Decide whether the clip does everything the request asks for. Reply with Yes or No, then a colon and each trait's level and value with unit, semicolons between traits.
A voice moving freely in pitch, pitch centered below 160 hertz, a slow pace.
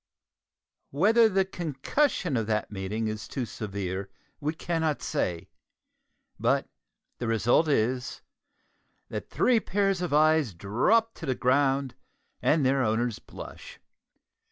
Yes: wide, 7.2 semitones; low, 135 Hz; slow, 125 wpm